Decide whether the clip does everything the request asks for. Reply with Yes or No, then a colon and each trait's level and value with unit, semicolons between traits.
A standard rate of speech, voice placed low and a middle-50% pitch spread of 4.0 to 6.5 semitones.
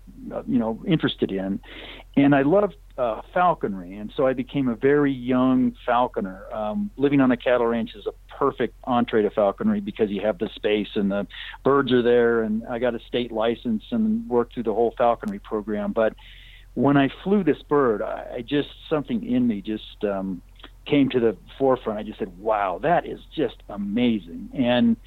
Yes: average, 190 wpm; low, 120 Hz; average, 4.7 semitones